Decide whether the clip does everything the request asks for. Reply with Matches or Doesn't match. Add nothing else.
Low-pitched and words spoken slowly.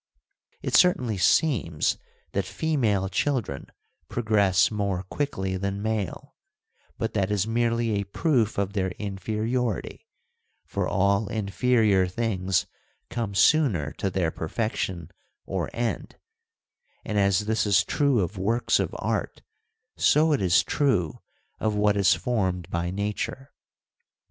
Matches